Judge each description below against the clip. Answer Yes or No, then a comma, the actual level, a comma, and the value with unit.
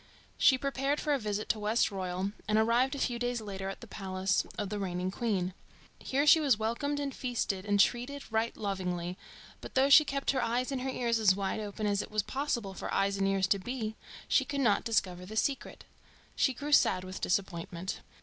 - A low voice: No, high, 215 Hz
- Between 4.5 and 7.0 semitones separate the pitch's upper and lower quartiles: Yes, average, 5.1 semitones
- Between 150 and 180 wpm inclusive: No, fast, 205 wpm